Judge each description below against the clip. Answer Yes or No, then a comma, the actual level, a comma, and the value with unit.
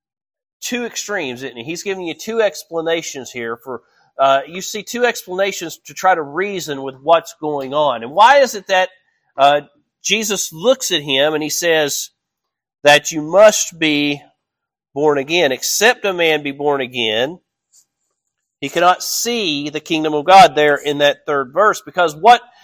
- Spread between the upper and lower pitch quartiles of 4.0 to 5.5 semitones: Yes, average, 4.8 semitones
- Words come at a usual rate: Yes, average, 165 wpm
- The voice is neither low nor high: Yes, medium, 160 Hz